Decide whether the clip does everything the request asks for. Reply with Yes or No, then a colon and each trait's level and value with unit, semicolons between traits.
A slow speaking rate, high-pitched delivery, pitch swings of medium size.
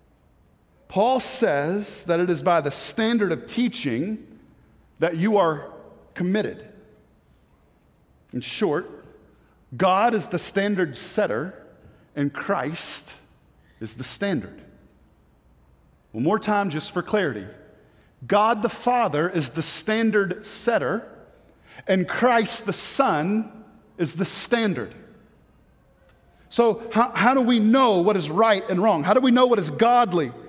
Yes: slow, 125 wpm; high, 205 Hz; average, 4.9 semitones